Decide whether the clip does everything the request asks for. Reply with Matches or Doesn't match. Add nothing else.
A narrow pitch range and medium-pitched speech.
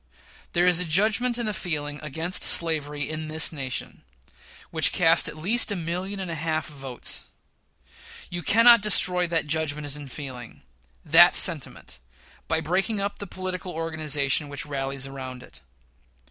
Doesn't match